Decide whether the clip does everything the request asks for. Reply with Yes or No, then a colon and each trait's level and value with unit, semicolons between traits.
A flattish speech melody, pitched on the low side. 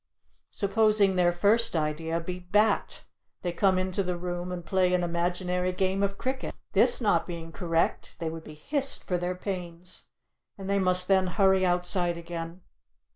No: narrow, 2.0 semitones; medium, 180 Hz